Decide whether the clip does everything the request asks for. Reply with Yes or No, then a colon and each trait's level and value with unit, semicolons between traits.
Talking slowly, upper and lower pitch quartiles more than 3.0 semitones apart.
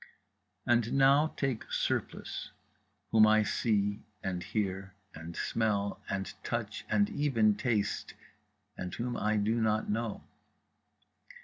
No: slow, 115 wpm; narrow, 2.6 semitones